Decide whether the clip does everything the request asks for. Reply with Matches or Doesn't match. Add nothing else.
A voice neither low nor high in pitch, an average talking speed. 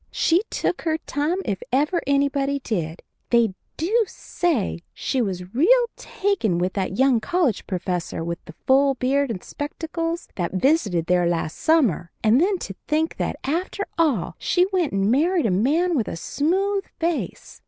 Doesn't match